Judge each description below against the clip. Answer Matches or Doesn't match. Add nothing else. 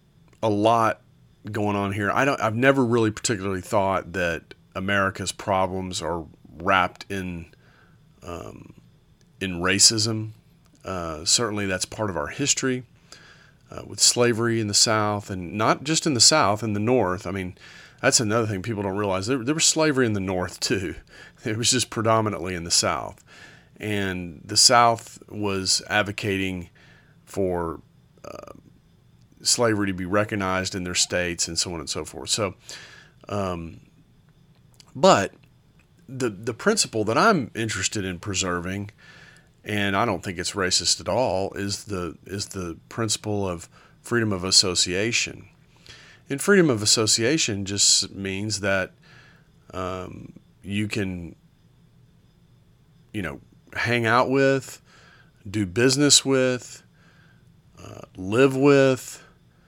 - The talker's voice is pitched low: Matches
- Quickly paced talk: Doesn't match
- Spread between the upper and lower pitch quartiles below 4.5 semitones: Doesn't match